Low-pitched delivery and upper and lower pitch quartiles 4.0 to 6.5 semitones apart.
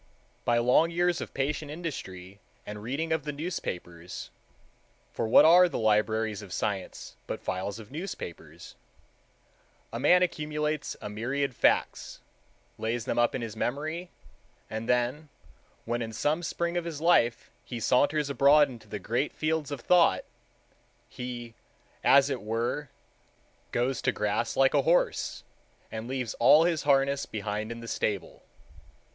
Yes: low, 125 Hz; wide, 5.6 semitones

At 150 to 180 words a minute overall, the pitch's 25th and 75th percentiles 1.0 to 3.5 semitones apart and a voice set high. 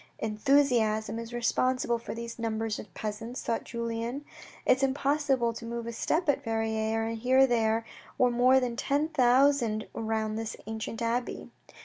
Yes: average, 155 wpm; narrow, 2.5 semitones; high, 235 Hz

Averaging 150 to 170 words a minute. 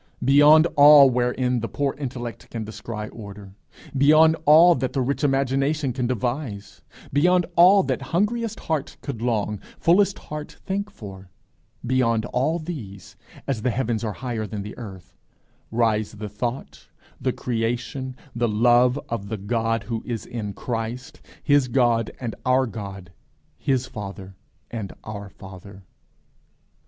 No: average, 140 wpm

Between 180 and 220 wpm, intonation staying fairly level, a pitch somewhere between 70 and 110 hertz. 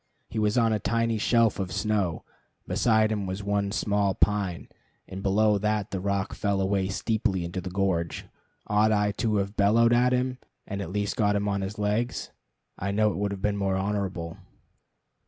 Yes: average, 190 wpm; narrow, 1.8 semitones; low, 100 Hz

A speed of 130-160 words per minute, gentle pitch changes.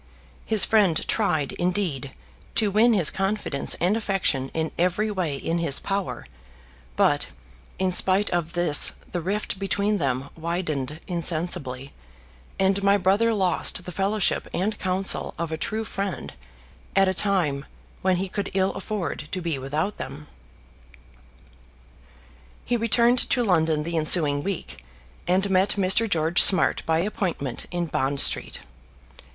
No: average, 140 wpm; average, 4.0 semitones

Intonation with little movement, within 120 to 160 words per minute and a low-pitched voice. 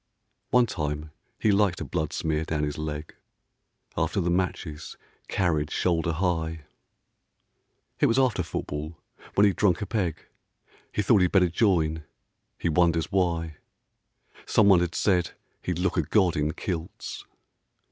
No: average, 3.4 semitones; average, 145 wpm; very low, 85 Hz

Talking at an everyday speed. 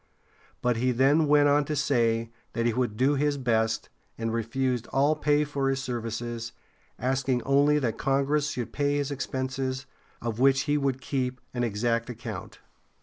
Yes: average, 165 wpm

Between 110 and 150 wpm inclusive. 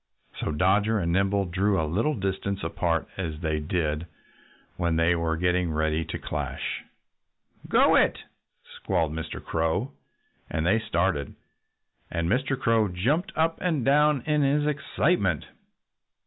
Yes: average, 140 wpm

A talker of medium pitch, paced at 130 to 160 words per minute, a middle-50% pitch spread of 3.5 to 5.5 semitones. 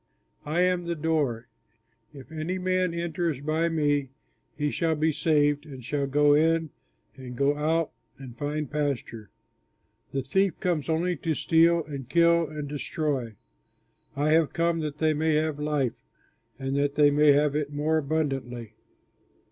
No: medium, 150 Hz; average, 155 wpm; narrow, 2.4 semitones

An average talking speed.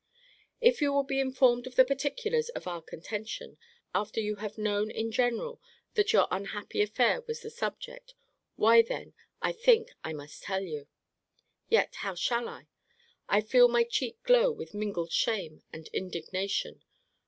Yes: average, 155 wpm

